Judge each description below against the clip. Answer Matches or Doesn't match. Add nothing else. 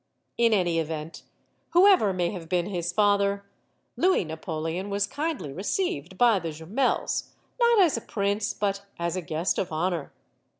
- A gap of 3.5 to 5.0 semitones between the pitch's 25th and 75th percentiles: Matches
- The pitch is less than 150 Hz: Doesn't match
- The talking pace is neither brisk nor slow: Matches